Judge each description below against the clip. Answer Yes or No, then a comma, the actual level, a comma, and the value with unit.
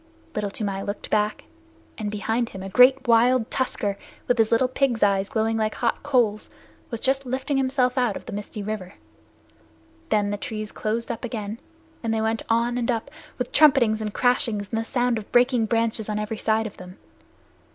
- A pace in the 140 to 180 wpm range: No, average, 190 wpm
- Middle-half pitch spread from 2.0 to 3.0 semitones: Yes, average, 2.7 semitones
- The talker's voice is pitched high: Yes, high, 225 Hz